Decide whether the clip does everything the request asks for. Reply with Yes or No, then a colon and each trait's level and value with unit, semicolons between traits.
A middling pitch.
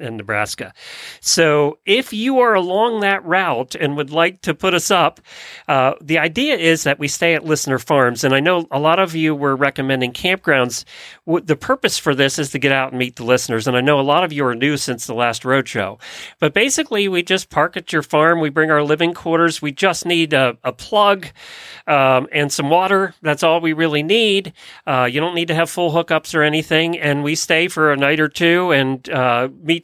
Yes: medium, 155 Hz